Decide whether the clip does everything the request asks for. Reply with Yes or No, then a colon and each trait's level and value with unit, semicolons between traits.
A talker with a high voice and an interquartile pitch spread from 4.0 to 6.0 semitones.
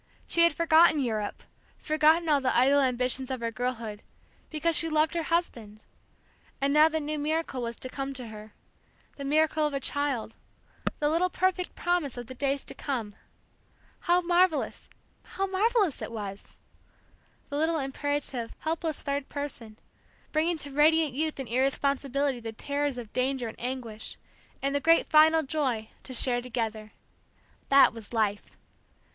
Yes: very high, 280 Hz; average, 4.5 semitones